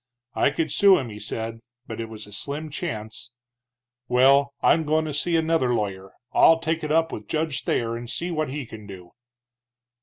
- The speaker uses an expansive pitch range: Yes, wide, 6.0 semitones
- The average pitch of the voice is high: No, low, 135 Hz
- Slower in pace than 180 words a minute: No, average, 190 wpm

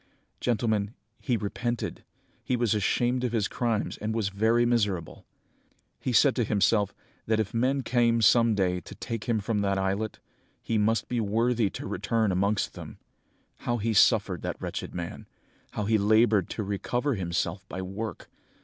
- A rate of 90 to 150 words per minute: No, average, 165 wpm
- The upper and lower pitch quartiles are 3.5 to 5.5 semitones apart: No, average, 2.8 semitones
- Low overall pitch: Yes, low, 110 Hz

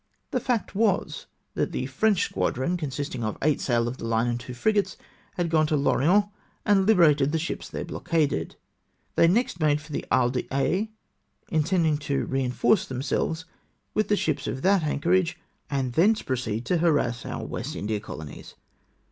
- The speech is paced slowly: No, average, 165 wpm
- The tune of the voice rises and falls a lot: Yes, wide, 5.9 semitones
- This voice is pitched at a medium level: Yes, medium, 150 Hz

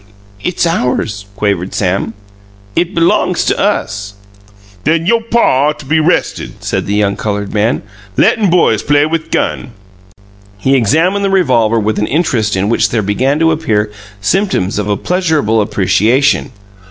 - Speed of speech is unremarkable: Yes, average, 155 wpm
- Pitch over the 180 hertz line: No, low, 125 Hz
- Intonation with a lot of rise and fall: Yes, wide, 7.8 semitones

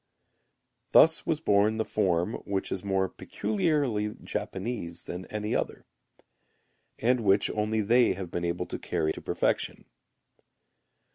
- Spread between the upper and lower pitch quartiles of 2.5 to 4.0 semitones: Yes, average, 3.6 semitones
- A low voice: Yes, low, 105 Hz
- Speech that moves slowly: Yes, slow, 130 wpm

